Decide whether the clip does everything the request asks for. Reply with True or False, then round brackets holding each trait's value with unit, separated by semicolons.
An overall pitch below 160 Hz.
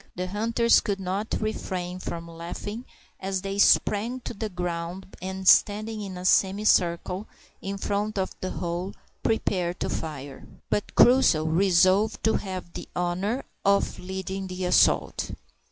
False (190 Hz)